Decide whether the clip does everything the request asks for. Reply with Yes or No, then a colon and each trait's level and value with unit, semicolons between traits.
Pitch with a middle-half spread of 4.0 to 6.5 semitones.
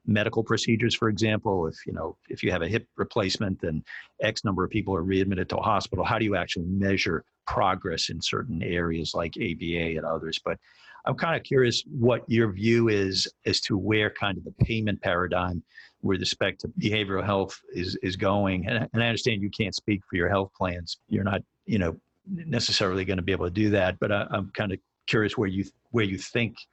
No: average, 3.3 semitones